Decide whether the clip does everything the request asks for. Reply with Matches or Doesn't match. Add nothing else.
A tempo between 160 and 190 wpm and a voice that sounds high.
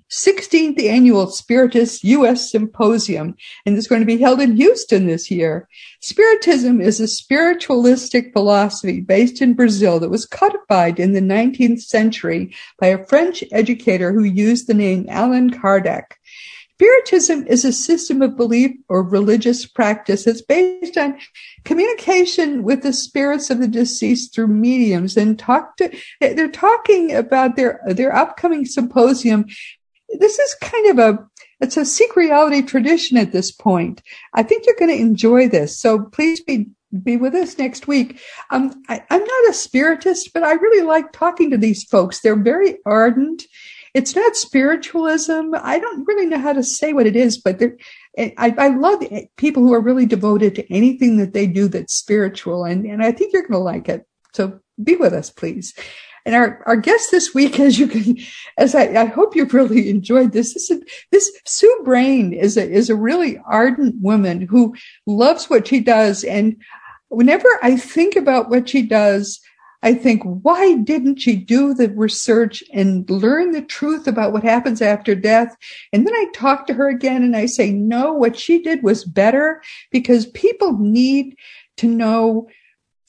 Matches